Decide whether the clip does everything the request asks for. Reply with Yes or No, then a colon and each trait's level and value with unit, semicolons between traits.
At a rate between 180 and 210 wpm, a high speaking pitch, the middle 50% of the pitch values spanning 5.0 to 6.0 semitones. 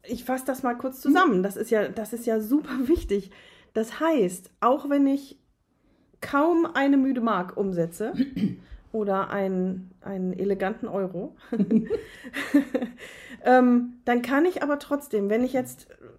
No: average, 135 wpm; high, 245 Hz; wide, 5.5 semitones